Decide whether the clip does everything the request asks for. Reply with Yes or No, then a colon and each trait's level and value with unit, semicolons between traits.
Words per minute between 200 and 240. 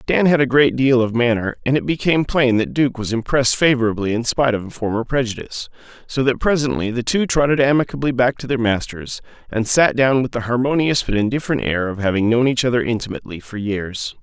Yes: fast, 205 wpm